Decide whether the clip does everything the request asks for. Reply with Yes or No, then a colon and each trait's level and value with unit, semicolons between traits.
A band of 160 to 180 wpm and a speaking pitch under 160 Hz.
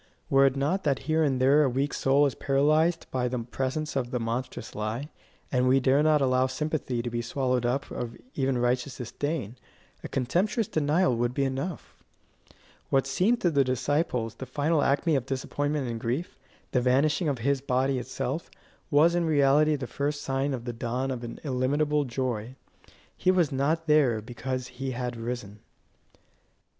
Yes: average, 175 wpm; low, 135 Hz